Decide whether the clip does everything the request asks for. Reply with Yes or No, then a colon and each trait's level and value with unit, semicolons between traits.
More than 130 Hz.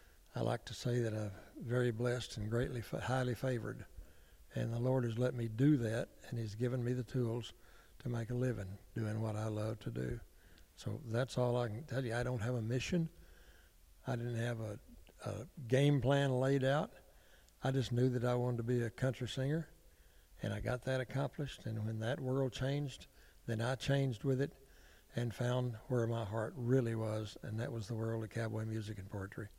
No: low, 120 Hz